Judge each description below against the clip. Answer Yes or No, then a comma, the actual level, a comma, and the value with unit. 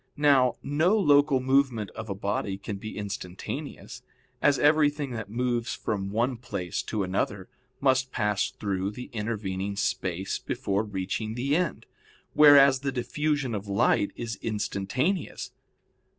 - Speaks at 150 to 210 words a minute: No, slow, 135 wpm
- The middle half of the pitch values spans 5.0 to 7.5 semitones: Yes, wide, 5.6 semitones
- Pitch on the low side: Yes, low, 115 Hz